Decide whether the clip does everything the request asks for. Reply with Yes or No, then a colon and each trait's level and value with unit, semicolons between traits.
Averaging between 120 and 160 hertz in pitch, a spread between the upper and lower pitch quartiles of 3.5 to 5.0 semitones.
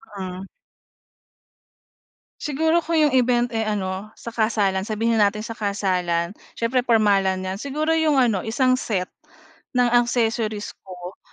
No: high, 220 Hz; average, 4.2 semitones